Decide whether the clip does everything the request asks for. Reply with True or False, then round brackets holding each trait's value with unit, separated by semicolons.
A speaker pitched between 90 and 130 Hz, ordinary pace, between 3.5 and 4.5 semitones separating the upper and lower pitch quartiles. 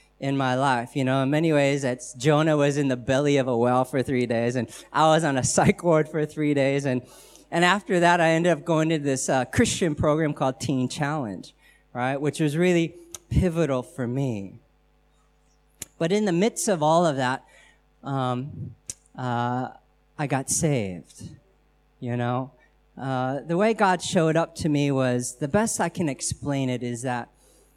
False (140 Hz; 185 wpm; 4.2 semitones)